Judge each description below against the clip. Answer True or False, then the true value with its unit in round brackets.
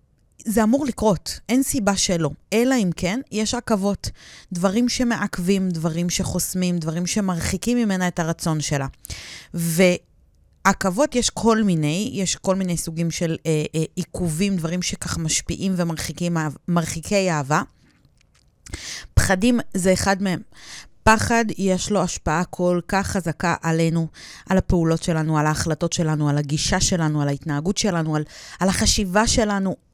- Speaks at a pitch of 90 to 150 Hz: False (180 Hz)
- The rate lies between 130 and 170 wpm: True (135 wpm)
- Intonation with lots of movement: False (3.7 semitones)